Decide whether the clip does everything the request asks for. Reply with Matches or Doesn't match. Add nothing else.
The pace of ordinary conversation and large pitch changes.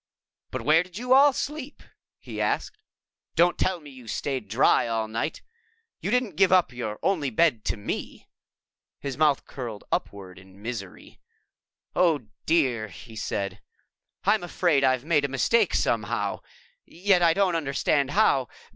Matches